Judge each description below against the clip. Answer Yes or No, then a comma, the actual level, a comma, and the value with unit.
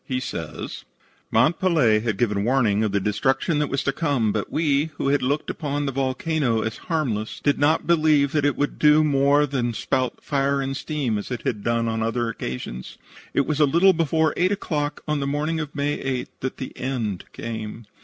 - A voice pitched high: No, low, 135 Hz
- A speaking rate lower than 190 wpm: No, fast, 205 wpm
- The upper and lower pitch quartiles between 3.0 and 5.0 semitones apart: Yes, average, 4.5 semitones